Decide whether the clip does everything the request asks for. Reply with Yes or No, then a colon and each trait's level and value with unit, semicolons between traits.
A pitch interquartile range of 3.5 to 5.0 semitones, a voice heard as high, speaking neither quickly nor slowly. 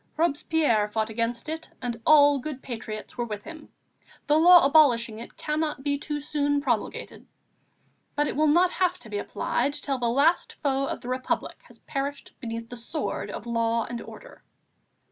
Yes: average, 4.5 semitones; very high, 275 Hz; average, 175 wpm